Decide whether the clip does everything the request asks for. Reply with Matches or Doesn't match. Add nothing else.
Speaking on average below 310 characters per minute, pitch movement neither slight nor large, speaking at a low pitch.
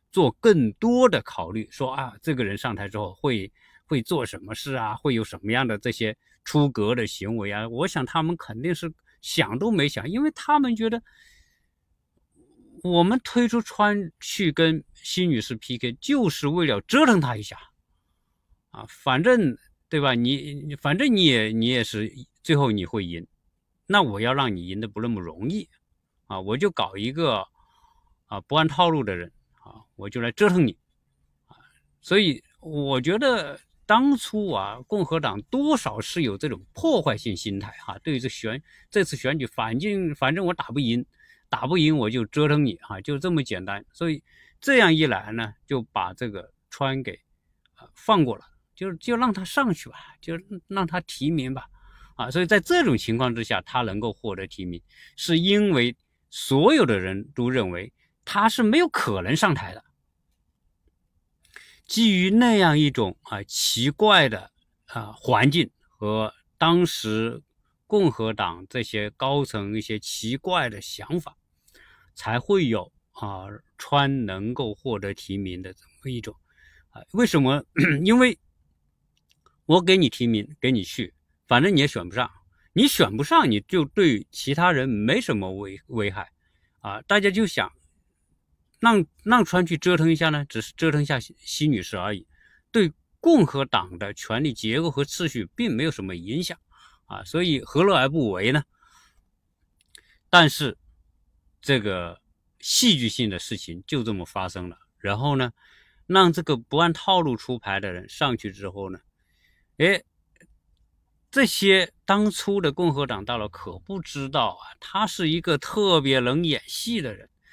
Doesn't match